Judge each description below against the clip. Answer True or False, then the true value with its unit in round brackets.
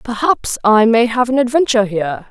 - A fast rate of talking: False (180 wpm)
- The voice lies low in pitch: False (235 Hz)